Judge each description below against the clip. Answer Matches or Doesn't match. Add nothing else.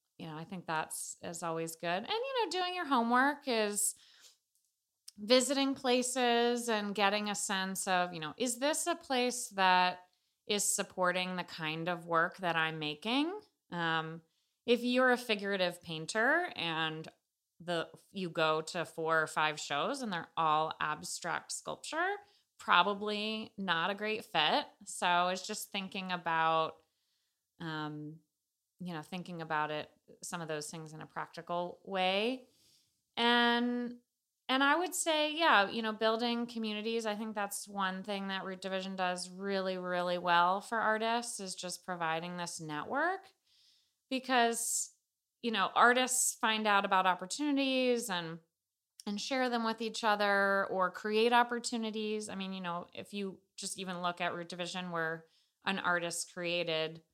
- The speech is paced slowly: Doesn't match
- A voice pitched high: Matches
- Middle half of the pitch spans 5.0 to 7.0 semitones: Matches